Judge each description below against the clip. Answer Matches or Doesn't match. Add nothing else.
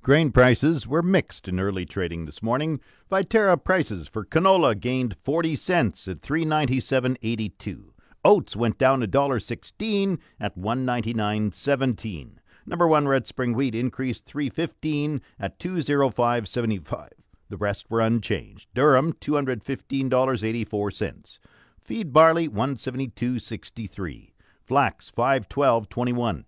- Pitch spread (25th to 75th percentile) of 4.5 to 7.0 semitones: Matches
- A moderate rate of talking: Matches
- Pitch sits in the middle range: Doesn't match